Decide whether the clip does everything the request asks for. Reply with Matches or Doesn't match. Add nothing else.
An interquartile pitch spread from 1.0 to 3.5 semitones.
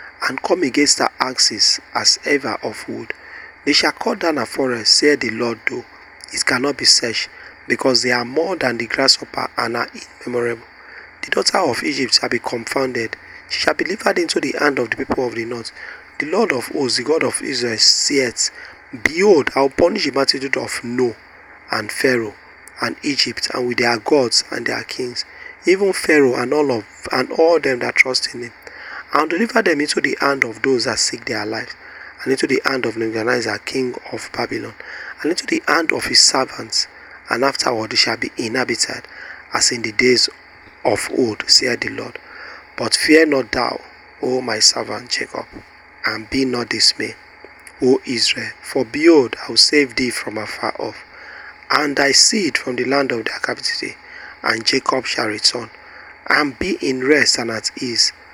Matches